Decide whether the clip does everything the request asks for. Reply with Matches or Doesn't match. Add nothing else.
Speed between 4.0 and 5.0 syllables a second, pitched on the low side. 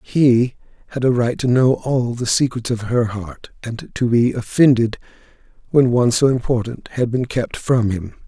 Matches